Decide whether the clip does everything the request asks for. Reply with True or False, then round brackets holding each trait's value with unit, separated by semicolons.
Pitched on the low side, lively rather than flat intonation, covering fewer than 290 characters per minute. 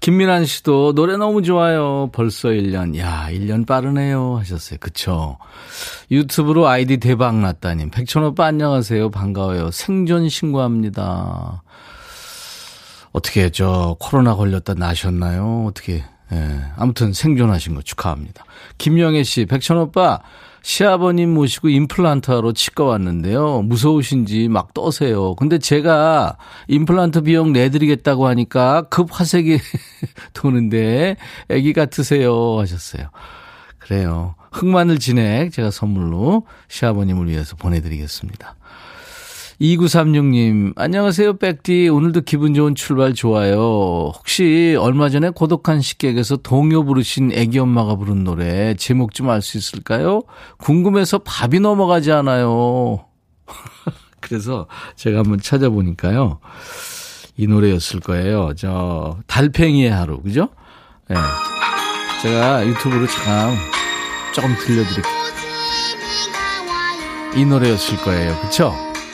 True (125 Hz; 7.6 semitones; 280 characters per minute)